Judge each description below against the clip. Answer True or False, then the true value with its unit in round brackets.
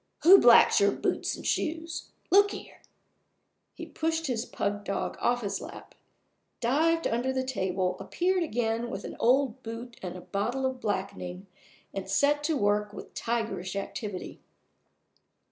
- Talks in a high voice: True (235 Hz)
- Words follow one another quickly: False (145 wpm)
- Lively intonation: True (6.0 semitones)